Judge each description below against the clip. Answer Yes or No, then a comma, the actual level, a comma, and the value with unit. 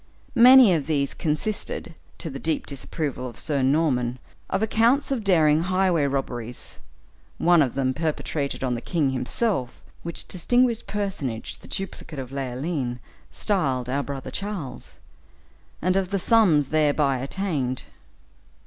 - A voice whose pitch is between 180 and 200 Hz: No, medium, 150 Hz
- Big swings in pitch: Yes, wide, 6.0 semitones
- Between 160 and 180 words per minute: No, slow, 135 wpm